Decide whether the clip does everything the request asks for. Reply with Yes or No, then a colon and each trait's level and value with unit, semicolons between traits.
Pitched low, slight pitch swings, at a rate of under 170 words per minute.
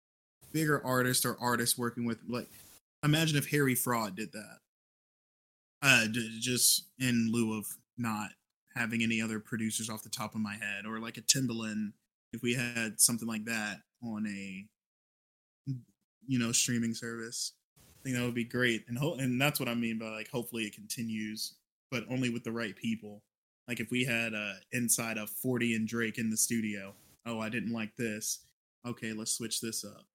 No: low, 115 Hz; narrow, 1.9 semitones; average, 185 wpm